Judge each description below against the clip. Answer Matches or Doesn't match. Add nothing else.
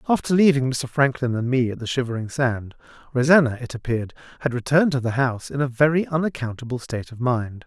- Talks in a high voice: Doesn't match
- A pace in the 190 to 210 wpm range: Matches